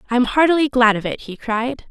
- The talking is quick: Yes, fast, 250 wpm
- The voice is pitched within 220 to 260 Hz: Yes, high, 245 Hz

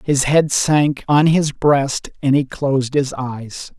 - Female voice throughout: No, male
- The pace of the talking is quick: No, average, 175 wpm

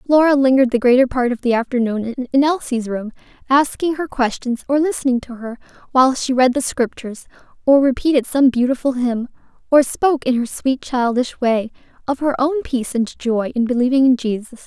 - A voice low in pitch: No, very high, 255 Hz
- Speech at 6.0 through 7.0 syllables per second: No, 5.6 syllables/s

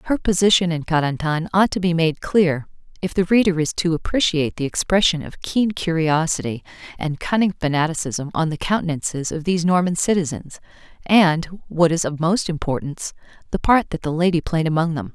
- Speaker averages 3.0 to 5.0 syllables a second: No, 5.5 syllables/s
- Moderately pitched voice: Yes, medium, 170 Hz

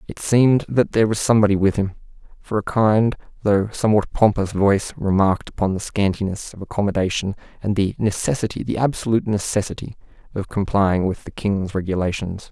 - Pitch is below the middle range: Yes, low, 100 Hz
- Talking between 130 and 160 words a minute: Yes, average, 155 wpm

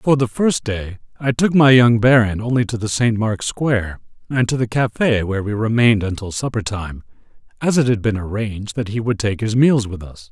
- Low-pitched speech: Yes, low, 115 Hz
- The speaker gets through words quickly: Yes, fast, 220 wpm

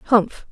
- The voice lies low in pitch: No, high, 215 Hz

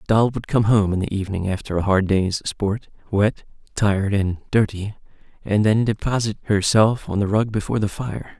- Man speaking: Yes, male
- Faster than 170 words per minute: Yes, average, 185 wpm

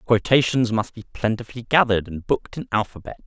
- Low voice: Yes, low, 110 Hz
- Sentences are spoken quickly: No, average, 165 wpm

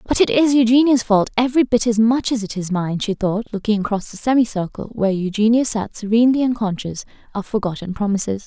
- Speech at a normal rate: Yes, average, 190 wpm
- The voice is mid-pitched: No, high, 220 Hz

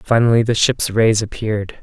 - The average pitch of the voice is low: Yes, low, 110 Hz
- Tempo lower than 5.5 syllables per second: Yes, 5.2 syllables/s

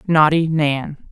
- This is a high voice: No, medium, 155 Hz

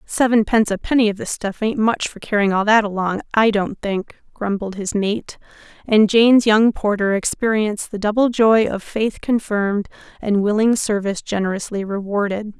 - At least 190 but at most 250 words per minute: No, average, 165 wpm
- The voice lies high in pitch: Yes, high, 210 Hz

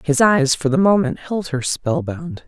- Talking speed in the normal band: Yes, average, 195 wpm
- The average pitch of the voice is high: Yes, high, 195 Hz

